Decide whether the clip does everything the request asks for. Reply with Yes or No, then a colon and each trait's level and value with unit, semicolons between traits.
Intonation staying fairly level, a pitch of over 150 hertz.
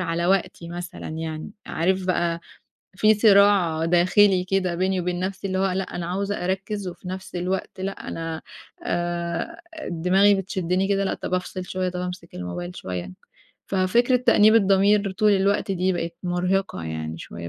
Yes: narrow, 2.1 semitones; medium, 185 Hz